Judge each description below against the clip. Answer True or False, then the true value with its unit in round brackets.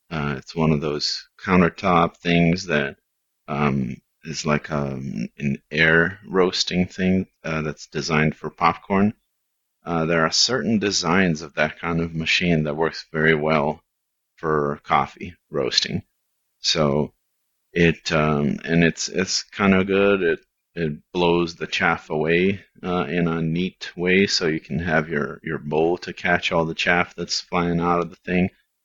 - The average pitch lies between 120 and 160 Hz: False (85 Hz)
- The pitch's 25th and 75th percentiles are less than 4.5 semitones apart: True (2.5 semitones)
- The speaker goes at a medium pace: True (160 wpm)